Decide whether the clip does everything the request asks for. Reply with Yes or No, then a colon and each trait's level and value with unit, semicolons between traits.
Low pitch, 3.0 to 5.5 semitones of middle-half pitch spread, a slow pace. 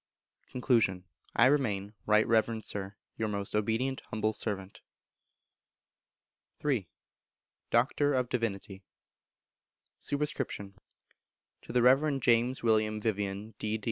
Yes: low, 110 Hz; average, 3.6 semitones; slow, 100 wpm